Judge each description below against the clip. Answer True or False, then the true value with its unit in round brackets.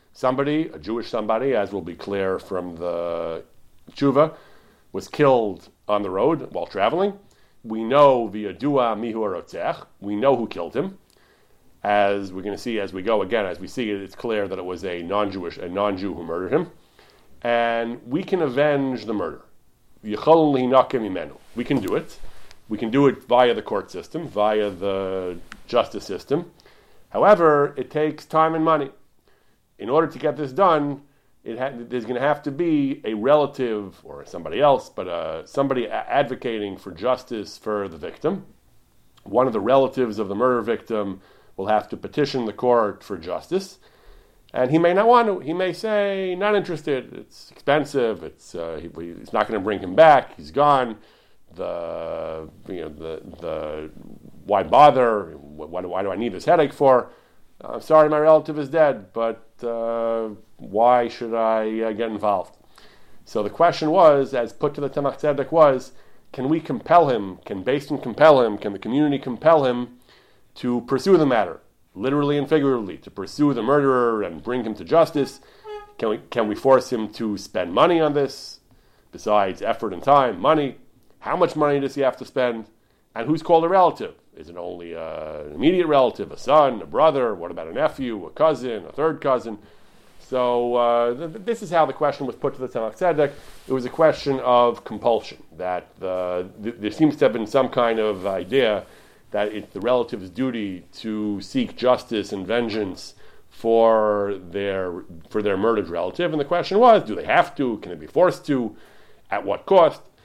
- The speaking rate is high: False (180 wpm)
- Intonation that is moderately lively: False (5.8 semitones)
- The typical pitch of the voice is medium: False (125 Hz)